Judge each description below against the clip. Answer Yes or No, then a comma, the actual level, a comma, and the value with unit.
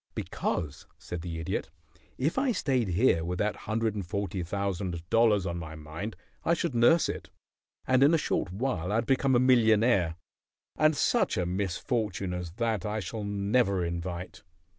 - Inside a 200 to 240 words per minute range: No, average, 165 wpm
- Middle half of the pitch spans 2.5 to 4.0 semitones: No, average, 5.2 semitones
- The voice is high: No, low, 100 Hz